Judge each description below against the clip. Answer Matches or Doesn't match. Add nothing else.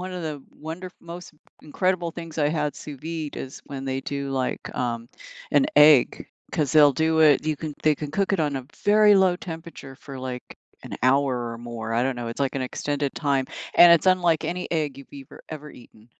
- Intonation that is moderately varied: Matches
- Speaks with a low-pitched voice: Doesn't match